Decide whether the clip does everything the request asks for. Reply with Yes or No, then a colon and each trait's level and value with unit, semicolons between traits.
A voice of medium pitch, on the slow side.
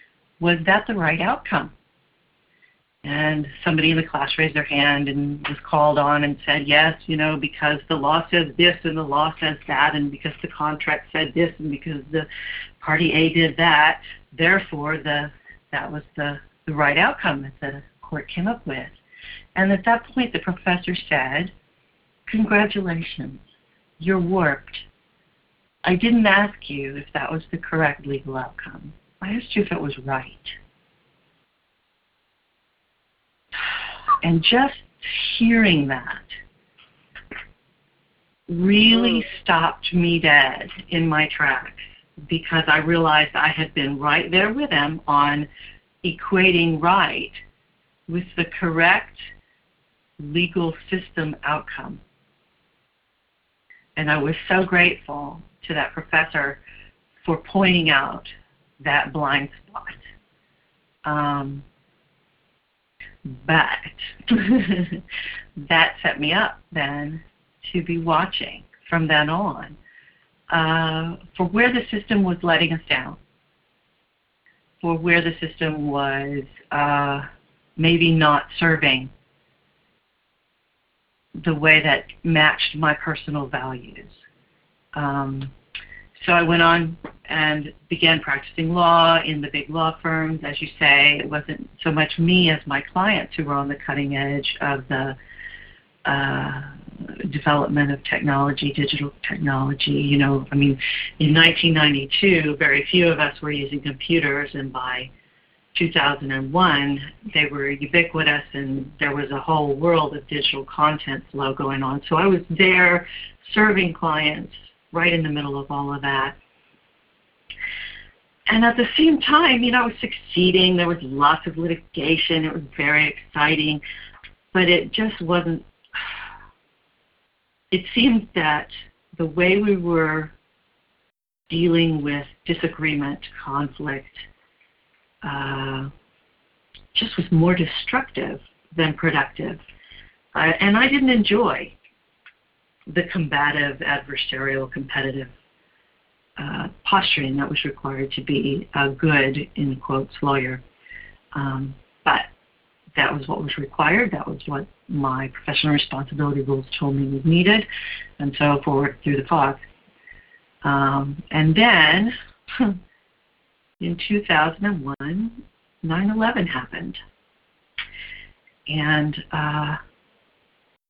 Yes: medium, 155 Hz; slow, 120 wpm